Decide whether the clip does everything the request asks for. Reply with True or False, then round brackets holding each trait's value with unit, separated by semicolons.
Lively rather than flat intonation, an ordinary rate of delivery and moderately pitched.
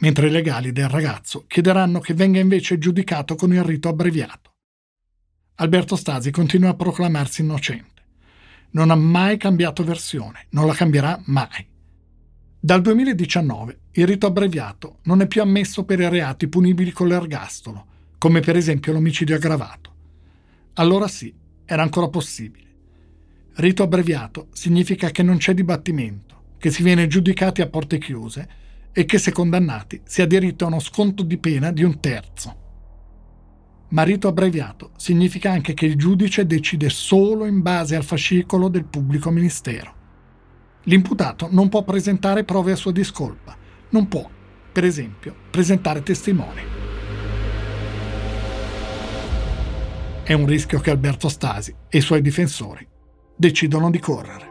True (9.0 semitones; 140 wpm; 160 Hz)